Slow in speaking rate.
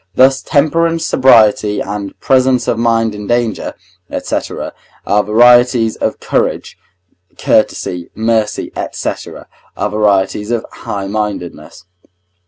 Yes: slow, 100 wpm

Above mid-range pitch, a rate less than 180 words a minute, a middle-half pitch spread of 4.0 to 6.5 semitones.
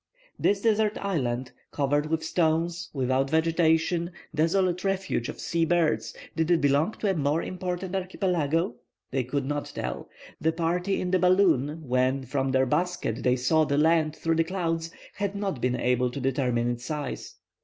No: medium, 160 Hz; average, 165 wpm; average, 4.7 semitones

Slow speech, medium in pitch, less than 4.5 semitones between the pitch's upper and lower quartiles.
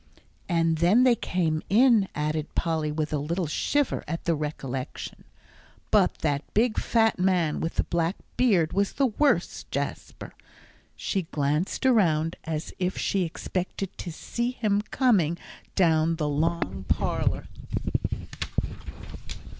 No: slow, 130 wpm; medium, 170 Hz; average, 4.8 semitones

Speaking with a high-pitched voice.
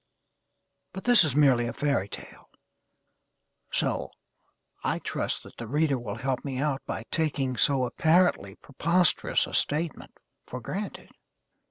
No: medium, 140 Hz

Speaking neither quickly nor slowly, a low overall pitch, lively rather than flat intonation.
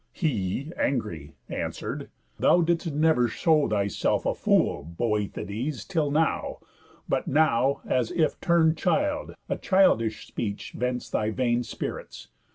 No: slow, 125 wpm; low, 130 Hz; wide, 6.7 semitones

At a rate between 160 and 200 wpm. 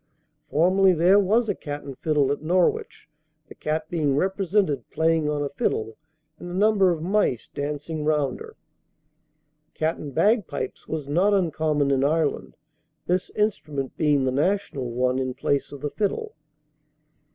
No: average, 150 wpm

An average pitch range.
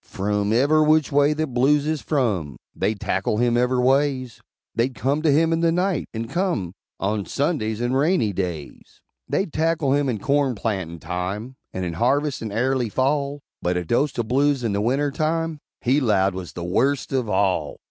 No: wide, 5.9 semitones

